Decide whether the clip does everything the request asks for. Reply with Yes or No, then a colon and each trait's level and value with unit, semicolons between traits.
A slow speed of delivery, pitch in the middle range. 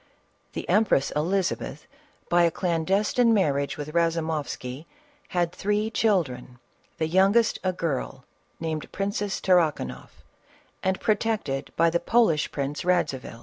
Yes: slow, 115 wpm; medium, 170 Hz